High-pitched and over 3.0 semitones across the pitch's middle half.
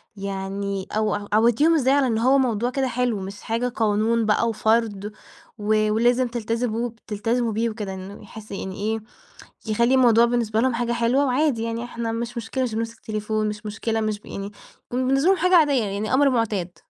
No: high, 230 Hz; narrow, 2.5 semitones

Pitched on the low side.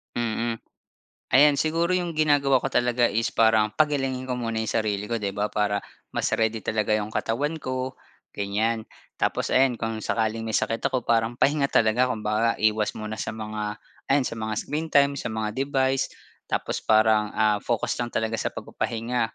Yes: low, 115 Hz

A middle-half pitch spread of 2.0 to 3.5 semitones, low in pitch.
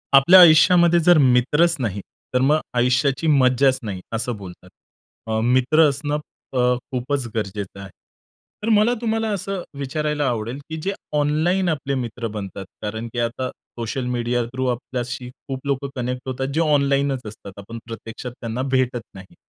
No: average, 4.1 semitones; low, 130 Hz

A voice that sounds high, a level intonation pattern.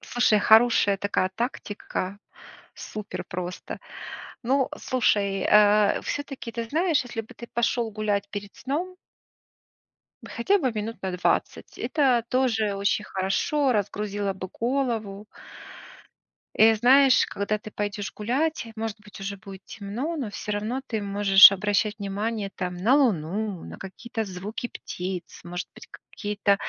No: high, 210 Hz; average, 3.2 semitones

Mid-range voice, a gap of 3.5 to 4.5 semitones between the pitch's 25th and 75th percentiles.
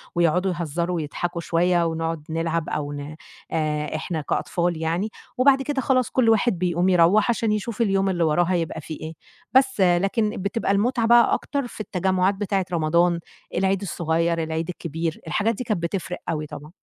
Yes: medium, 175 Hz; average, 4.0 semitones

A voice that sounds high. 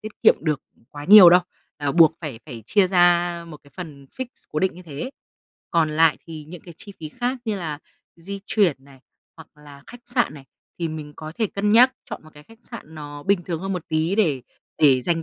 No: medium, 165 Hz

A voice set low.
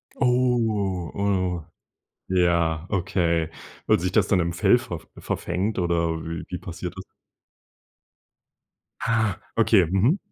Yes: very low, 95 Hz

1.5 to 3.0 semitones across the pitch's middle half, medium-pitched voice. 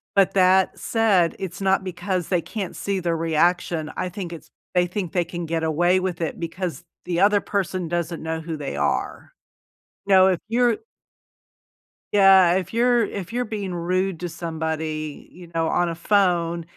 Yes: narrow, 2.5 semitones; medium, 180 Hz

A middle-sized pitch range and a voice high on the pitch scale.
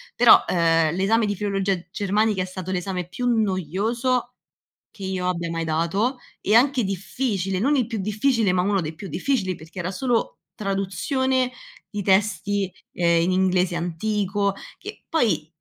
Yes: average, 3.7 semitones; high, 195 Hz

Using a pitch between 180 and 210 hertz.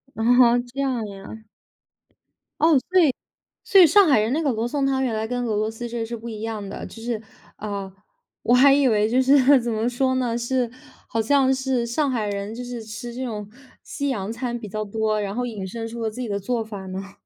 No: high, 235 Hz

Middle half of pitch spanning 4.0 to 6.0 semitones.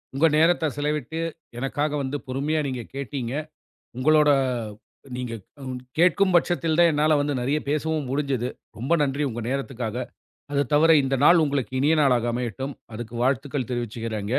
No: average, 3.5 semitones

